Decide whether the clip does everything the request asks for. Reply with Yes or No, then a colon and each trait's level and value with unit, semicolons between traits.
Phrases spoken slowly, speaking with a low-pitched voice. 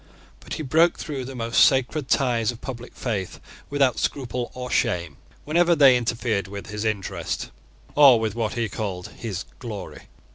No: average, 160 wpm; low, 120 Hz